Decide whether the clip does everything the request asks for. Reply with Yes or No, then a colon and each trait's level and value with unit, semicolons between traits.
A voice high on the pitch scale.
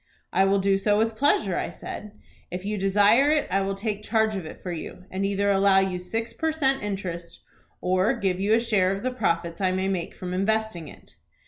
Yes: high, 195 Hz